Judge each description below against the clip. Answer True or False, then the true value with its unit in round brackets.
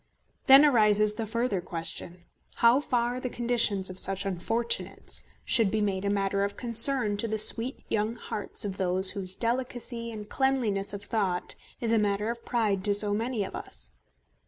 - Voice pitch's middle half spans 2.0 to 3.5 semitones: True (3.0 semitones)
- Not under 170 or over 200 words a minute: True (175 wpm)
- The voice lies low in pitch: False (215 Hz)